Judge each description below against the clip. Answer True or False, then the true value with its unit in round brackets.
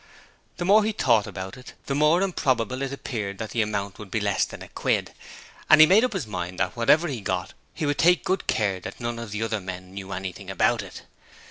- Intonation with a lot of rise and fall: True (7.5 semitones)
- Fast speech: True (235 wpm)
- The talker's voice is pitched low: True (115 Hz)